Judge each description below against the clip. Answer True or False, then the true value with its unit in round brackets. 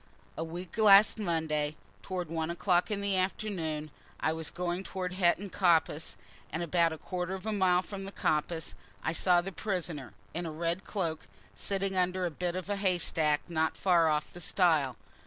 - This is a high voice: False (175 Hz)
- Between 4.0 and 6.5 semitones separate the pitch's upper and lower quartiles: False (2.8 semitones)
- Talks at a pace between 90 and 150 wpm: False (180 wpm)